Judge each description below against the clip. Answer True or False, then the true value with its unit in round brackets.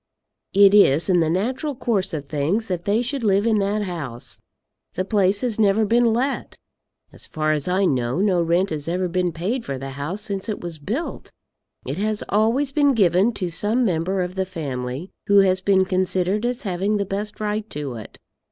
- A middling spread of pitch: True (4.1 semitones)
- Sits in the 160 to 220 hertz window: True (190 Hz)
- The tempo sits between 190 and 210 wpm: True (200 wpm)